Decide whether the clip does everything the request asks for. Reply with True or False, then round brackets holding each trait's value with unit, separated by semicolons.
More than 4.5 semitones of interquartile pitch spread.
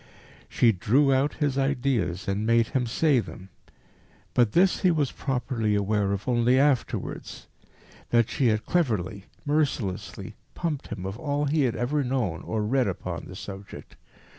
True (5.1 semitones)